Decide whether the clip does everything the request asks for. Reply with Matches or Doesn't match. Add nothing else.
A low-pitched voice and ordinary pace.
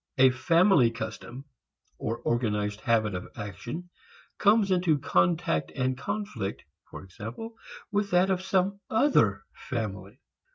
Doesn't match